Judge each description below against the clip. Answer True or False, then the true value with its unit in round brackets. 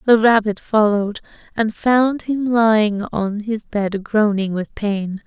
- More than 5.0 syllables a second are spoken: False (3.8 syllables/s)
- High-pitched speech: True (215 Hz)